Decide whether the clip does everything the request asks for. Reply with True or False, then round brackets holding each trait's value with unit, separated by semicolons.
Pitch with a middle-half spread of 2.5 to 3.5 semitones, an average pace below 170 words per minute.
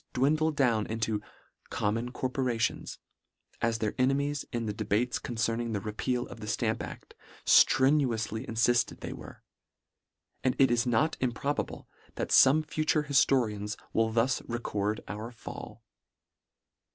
True (3.0 semitones; 135 wpm)